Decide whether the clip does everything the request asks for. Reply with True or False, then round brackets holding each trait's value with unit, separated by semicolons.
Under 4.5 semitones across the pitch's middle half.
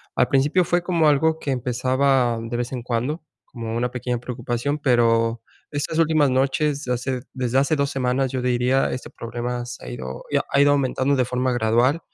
True (2.7 semitones)